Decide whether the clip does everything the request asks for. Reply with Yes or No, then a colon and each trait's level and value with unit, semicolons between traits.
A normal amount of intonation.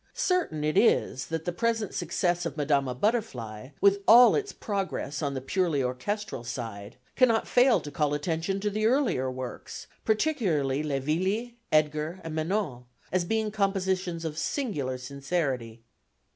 No: wide, 7.2 semitones